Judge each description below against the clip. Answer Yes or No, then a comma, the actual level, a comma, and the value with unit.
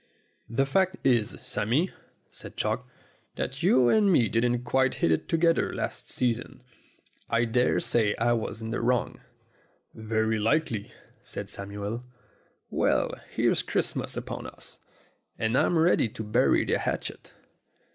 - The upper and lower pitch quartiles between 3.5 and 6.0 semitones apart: No, average, 3.1 semitones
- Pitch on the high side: No, low, 120 Hz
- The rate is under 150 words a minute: Yes, slow, 135 wpm